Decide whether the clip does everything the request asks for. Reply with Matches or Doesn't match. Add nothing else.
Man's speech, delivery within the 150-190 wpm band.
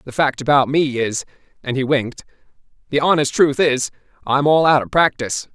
Matches